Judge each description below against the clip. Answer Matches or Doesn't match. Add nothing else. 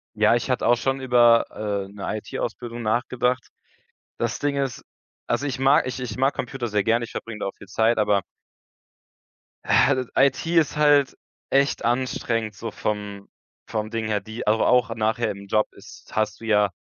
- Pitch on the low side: Matches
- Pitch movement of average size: Matches